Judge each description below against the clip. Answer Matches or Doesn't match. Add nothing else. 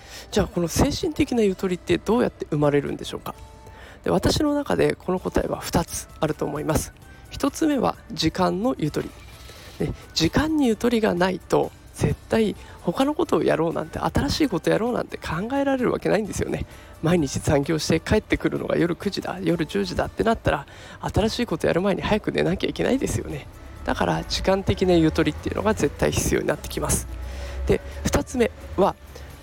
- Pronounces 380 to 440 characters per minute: Doesn't match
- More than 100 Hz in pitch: Matches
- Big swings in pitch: Matches